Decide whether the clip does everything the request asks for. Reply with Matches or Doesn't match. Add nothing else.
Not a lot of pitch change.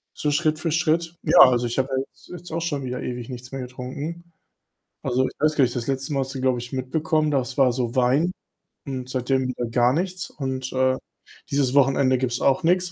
Doesn't match